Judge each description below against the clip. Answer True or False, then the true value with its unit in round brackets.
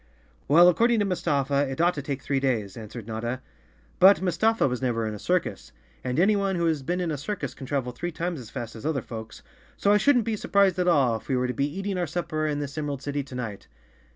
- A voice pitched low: False (145 Hz)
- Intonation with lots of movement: True (6.0 semitones)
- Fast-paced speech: True (245 wpm)